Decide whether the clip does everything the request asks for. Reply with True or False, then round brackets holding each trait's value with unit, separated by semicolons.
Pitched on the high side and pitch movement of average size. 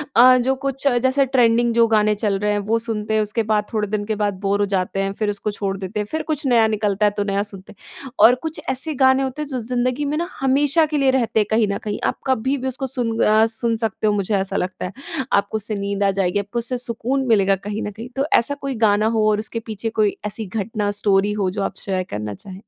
True (220 Hz; 3.7 semitones)